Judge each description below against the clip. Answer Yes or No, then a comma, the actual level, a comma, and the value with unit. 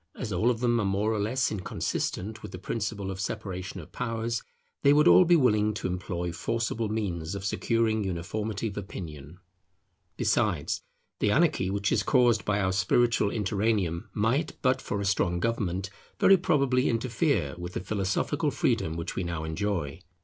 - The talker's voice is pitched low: Yes, low, 105 Hz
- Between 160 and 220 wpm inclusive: Yes, average, 170 wpm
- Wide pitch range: No, average, 3.8 semitones